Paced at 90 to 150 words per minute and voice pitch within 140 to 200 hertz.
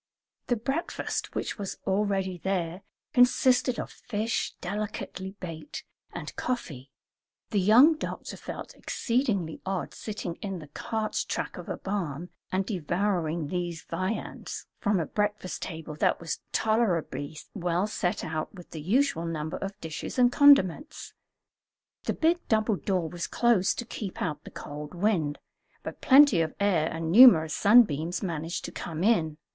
Yes: average, 145 wpm; high, 190 Hz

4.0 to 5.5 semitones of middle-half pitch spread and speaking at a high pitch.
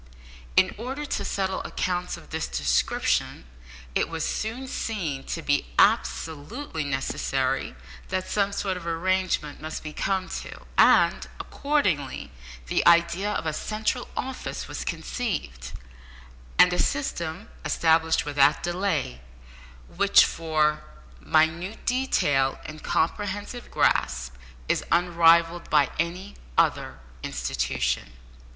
No: average, 5.1 semitones; medium, 165 Hz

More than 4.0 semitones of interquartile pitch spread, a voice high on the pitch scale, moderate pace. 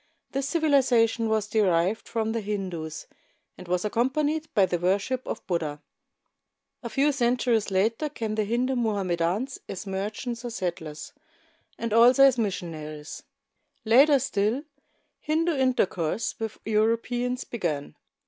No: average, 4.9 semitones; high, 220 Hz; slow, 130 wpm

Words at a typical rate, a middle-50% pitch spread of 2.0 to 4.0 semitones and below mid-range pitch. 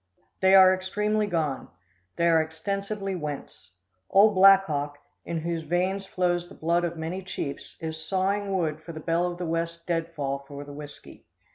No: average, 165 wpm; average, 3.1 semitones; medium, 170 Hz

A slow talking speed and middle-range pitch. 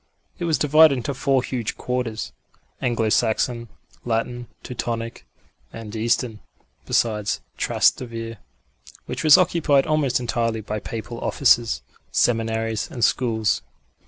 No: slow, 110 wpm; low, 120 Hz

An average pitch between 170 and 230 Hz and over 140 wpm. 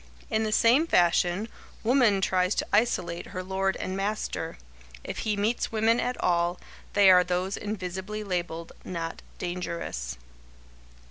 No: high, 190 Hz; slow, 135 wpm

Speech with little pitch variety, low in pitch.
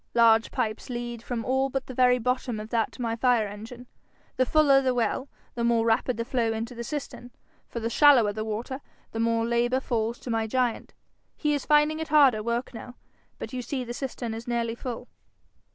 No: narrow, 2.1 semitones; high, 240 Hz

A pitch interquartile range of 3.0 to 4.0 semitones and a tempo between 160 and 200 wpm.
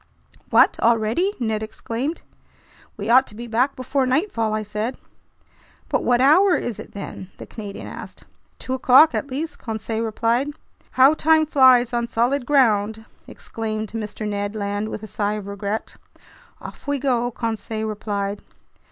No: average, 3.5 semitones; average, 150 wpm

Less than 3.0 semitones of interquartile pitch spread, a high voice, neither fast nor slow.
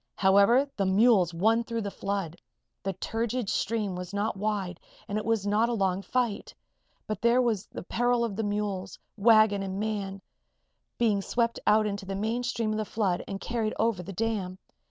Yes: narrow, 2.6 semitones; high, 210 Hz; average, 180 wpm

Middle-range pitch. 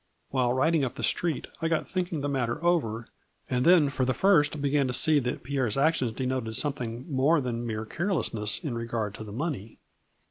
No: low, 130 Hz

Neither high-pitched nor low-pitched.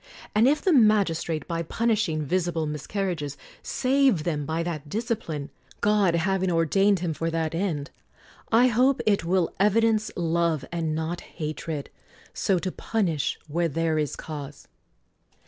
Yes: medium, 170 Hz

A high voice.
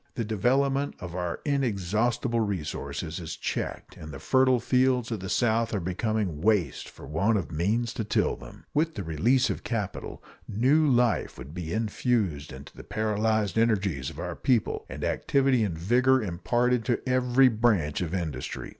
No: low, 110 Hz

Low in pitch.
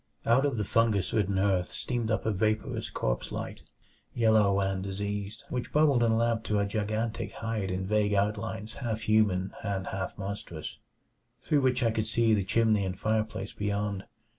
Yes: low, 105 Hz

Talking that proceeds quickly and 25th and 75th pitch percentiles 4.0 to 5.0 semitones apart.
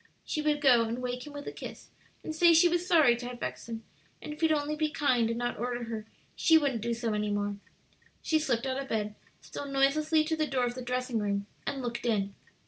Yes: fast, 240 wpm; average, 4.7 semitones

